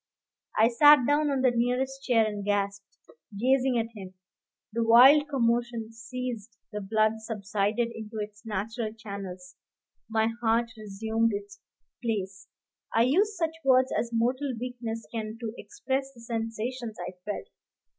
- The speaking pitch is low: No, high, 230 Hz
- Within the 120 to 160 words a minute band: Yes, average, 140 wpm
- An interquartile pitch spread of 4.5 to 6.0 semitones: No, average, 2.8 semitones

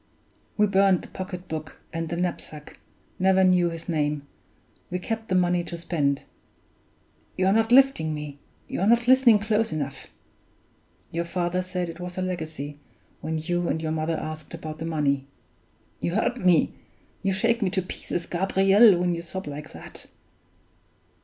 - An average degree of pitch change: Yes, average, 3.3 semitones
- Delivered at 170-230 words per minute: No, average, 160 wpm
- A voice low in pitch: No, medium, 175 Hz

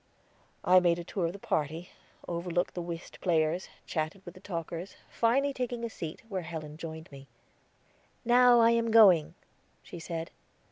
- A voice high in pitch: No, medium, 175 Hz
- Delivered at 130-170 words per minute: Yes, average, 160 wpm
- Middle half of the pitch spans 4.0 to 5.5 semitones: Yes, average, 5.0 semitones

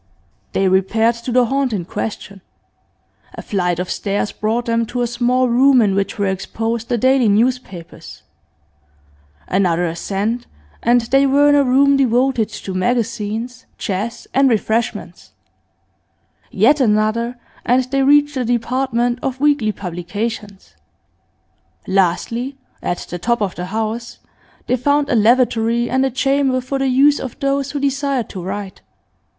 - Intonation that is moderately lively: Yes, average, 4.1 semitones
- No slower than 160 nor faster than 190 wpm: No, average, 145 wpm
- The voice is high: Yes, high, 235 Hz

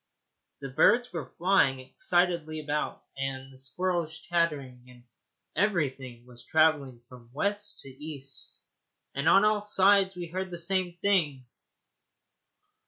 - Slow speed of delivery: Yes, slow, 125 wpm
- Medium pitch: Yes, medium, 155 Hz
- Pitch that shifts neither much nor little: No, wide, 5.8 semitones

